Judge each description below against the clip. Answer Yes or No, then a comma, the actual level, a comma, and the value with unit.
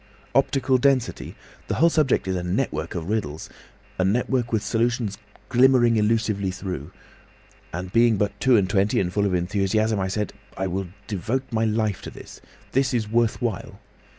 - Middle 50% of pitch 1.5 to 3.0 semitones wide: No, average, 3.8 semitones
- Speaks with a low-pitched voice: Yes, low, 110 Hz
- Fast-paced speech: No, average, 165 wpm